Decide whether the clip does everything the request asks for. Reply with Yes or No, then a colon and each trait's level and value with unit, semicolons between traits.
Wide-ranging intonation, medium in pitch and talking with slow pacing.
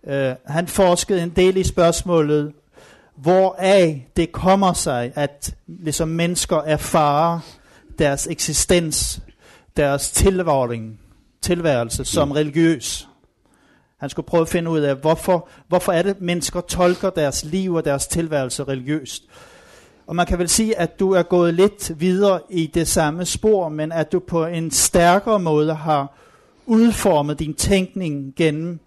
No: average, 3.3 semitones; medium, 165 Hz; slow, 135 wpm